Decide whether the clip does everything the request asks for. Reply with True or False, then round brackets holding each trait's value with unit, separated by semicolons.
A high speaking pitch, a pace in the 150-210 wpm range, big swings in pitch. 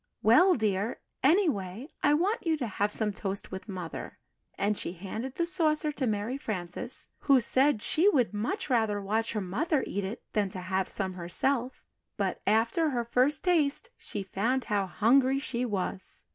True (225 Hz; 175 wpm; 5.8 semitones)